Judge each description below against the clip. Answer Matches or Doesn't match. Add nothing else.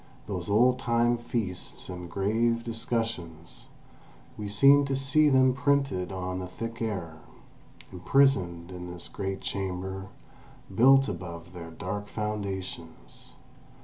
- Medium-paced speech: Doesn't match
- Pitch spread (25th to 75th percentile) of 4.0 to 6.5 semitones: Matches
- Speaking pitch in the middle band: Doesn't match